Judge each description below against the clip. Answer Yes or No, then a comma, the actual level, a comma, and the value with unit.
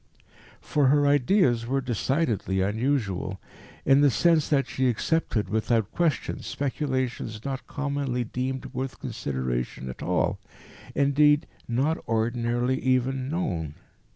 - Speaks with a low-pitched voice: Yes, low, 130 Hz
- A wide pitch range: No, average, 3.9 semitones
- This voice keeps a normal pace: No, slow, 115 wpm